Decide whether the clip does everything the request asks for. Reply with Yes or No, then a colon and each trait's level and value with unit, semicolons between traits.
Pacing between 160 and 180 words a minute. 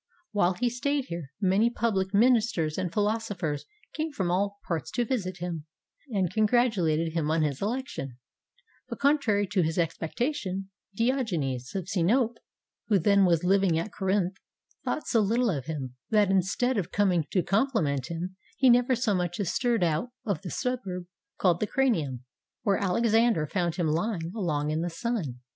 Yes: average, 170 wpm